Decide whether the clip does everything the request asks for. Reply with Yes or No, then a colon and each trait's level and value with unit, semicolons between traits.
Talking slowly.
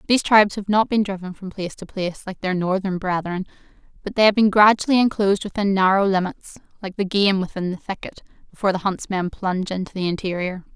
No: average, 200 wpm